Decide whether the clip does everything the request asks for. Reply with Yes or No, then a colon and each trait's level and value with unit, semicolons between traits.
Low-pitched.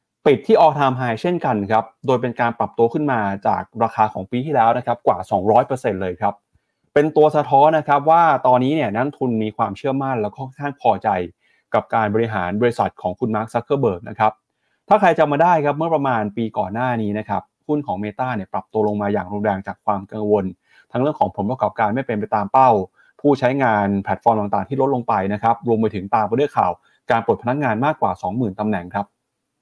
Yes: low, 115 Hz